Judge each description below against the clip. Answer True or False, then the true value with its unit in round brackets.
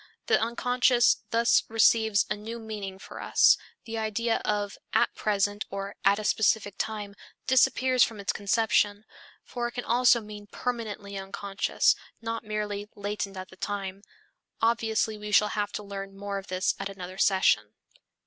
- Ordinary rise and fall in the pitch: False (2.2 semitones)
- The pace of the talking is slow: False (160 wpm)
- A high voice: True (210 Hz)